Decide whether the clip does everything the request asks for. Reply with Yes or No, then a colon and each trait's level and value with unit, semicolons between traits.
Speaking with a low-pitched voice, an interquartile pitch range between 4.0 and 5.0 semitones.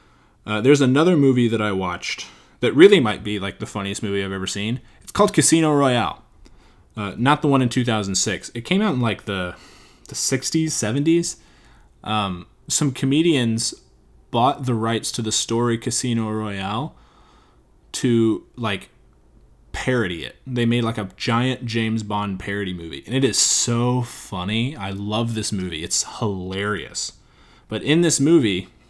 Yes: low, 110 Hz; average, 4.5 semitones